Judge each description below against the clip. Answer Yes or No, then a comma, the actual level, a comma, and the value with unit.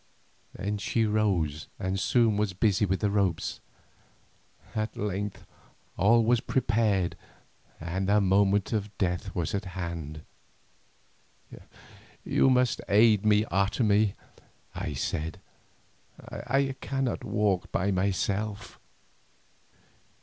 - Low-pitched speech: Yes, low, 100 Hz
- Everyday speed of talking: No, slow, 105 wpm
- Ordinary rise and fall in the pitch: No, narrow, 2.3 semitones